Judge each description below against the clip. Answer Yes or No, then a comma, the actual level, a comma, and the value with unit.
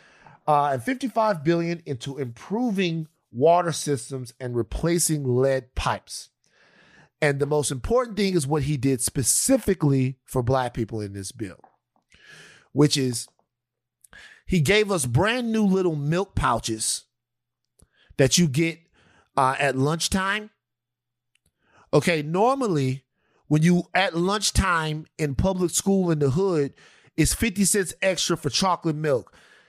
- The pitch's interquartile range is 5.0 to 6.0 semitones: Yes, wide, 5.6 semitones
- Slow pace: Yes, slow, 125 wpm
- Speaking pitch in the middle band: Yes, medium, 150 Hz